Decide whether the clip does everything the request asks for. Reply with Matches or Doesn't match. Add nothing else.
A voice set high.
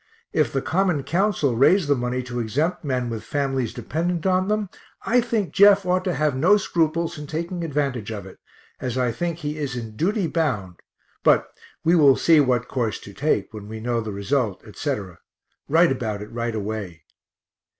Doesn't match